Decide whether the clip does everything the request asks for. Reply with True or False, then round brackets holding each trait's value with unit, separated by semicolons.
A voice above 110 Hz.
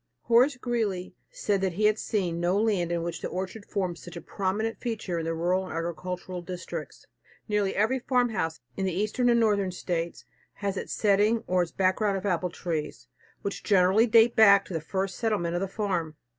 True (190 Hz)